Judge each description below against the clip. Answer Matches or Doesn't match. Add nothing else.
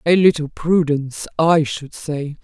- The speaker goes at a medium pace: Matches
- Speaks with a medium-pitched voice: Matches